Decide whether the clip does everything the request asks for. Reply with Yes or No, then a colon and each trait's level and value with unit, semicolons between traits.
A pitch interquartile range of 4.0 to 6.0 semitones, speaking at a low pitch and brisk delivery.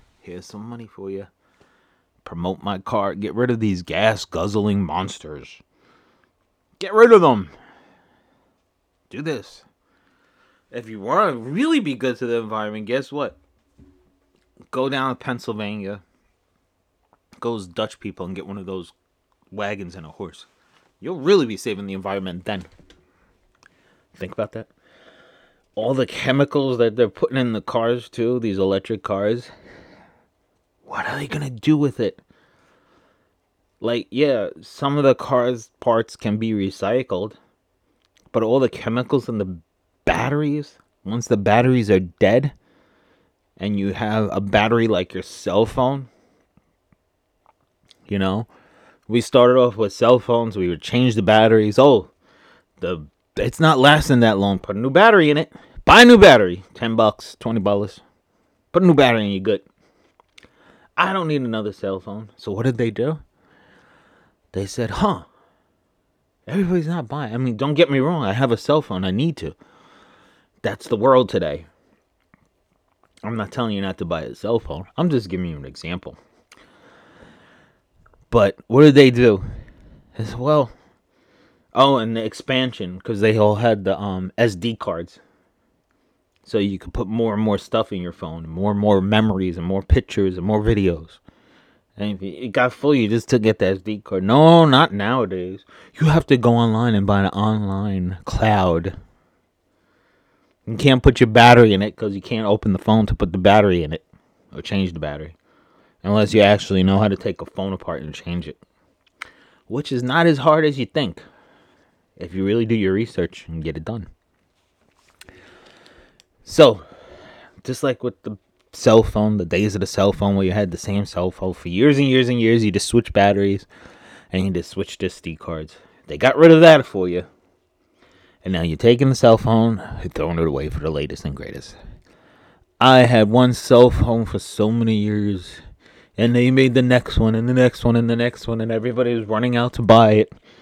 No: average, 4.5 semitones; low, 105 Hz; average, 175 wpm